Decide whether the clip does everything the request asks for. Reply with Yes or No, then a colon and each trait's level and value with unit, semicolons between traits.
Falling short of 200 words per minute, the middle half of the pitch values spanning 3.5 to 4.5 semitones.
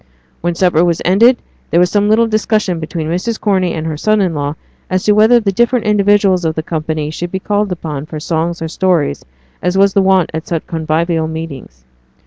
No: fast, 205 wpm; average, 4.1 semitones